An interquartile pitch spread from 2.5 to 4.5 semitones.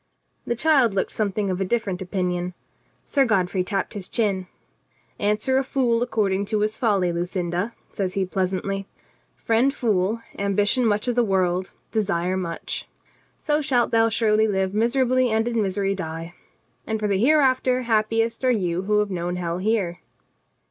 Yes: average, 3.8 semitones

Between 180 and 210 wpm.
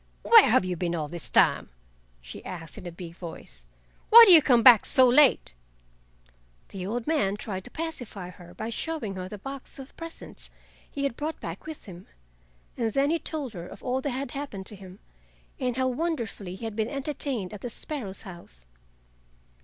Yes: average, 195 wpm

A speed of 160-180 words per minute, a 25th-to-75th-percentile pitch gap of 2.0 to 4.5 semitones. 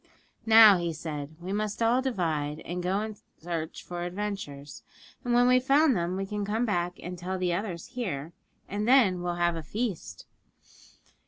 Yes: average, 175 wpm; average, 4.2 semitones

